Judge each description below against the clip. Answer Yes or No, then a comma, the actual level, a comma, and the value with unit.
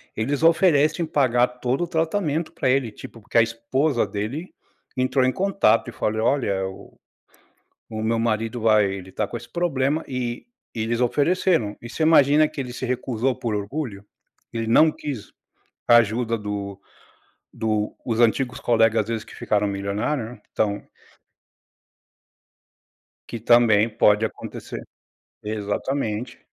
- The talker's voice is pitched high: No, low, 120 Hz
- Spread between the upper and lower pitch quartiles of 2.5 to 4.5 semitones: Yes, average, 4.2 semitones